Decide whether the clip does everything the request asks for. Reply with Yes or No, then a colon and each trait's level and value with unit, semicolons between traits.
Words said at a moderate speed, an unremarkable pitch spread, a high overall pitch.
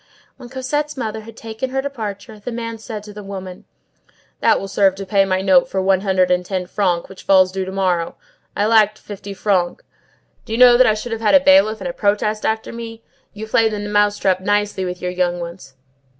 No: fast, 220 wpm; average, 3.0 semitones; high, 205 Hz